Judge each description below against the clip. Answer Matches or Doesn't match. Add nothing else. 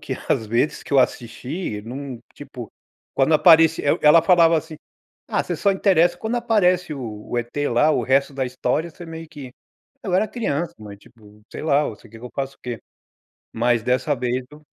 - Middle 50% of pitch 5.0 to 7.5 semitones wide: Matches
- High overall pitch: Doesn't match